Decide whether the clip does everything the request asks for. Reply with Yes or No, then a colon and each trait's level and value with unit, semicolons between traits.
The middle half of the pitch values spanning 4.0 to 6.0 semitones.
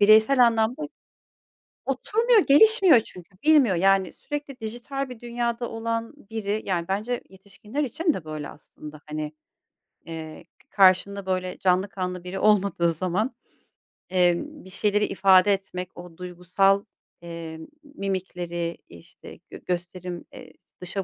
Yes: average, 4.7 semitones